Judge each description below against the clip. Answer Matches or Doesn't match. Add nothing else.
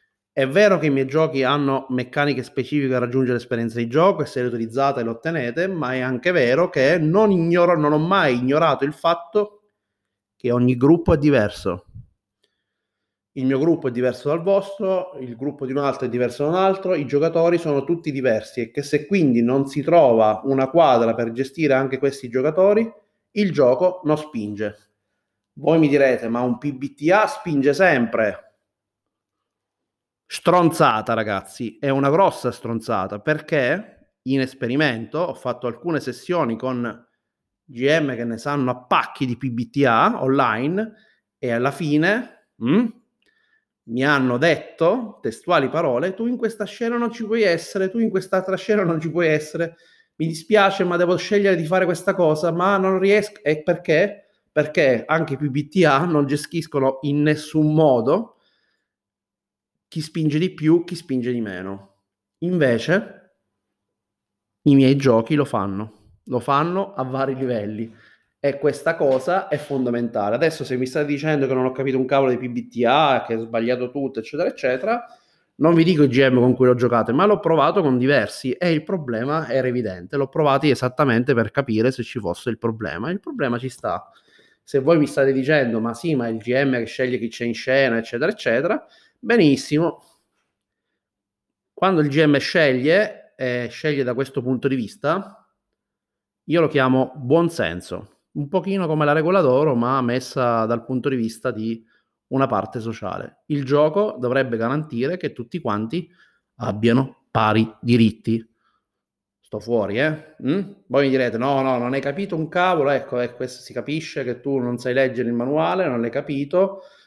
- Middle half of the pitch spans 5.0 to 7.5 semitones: Matches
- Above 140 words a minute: Matches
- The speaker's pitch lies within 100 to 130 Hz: Doesn't match